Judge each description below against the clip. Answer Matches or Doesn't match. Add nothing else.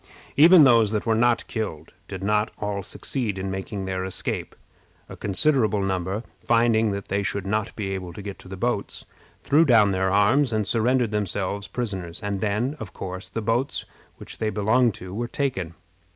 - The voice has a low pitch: Matches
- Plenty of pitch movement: Doesn't match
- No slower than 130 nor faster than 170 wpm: Doesn't match